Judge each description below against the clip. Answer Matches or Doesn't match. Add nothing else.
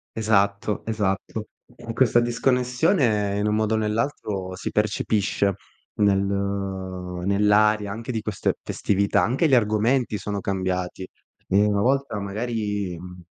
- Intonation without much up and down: Matches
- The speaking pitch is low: Matches